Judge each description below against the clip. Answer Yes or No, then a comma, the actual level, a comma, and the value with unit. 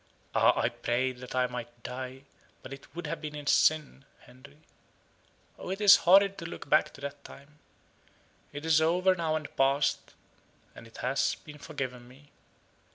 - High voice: No, medium, 140 Hz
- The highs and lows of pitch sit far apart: No, average, 3.5 semitones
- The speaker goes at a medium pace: Yes, average, 170 wpm